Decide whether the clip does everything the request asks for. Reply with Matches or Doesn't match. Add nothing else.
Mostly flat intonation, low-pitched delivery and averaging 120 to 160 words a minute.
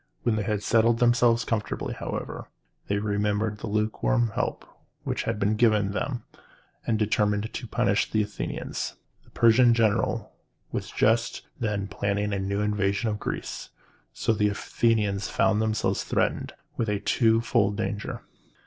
Matches